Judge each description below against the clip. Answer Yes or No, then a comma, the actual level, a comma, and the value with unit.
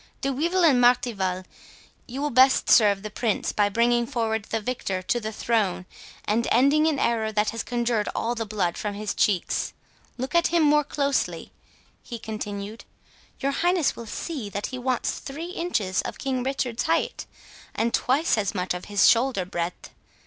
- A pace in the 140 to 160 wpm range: No, average, 170 wpm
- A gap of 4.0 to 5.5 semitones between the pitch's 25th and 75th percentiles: Yes, average, 4.5 semitones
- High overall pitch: Yes, high, 235 Hz